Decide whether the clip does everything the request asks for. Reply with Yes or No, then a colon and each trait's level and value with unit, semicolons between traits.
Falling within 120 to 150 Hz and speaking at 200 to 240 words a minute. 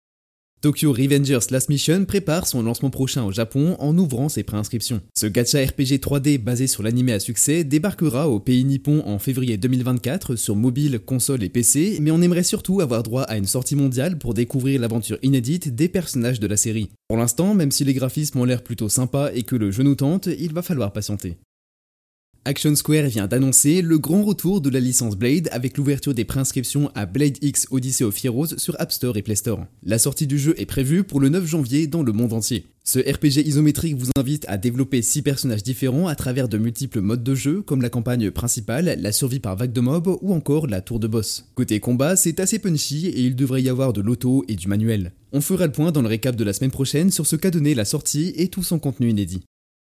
Yes: low, 135 Hz; fast, 220 wpm